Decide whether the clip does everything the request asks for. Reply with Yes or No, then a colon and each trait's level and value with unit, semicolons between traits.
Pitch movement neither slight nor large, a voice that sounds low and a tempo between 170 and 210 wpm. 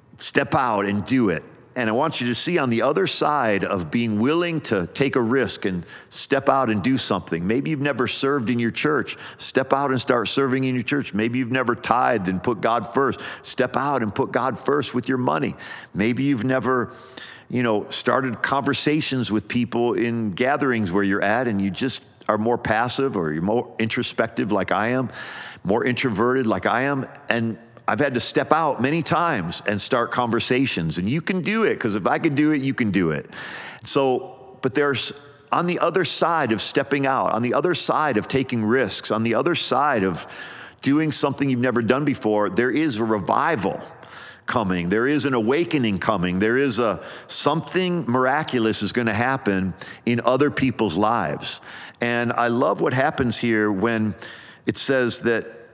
Yes: average, 3.6 semitones; low, 125 Hz; average, 195 wpm